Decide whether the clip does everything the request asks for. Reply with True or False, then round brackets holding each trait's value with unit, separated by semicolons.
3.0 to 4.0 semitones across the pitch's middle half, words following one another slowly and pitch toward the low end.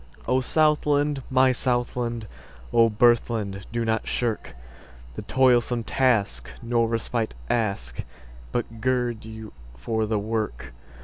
True (3.4 semitones; 100 wpm; 115 Hz)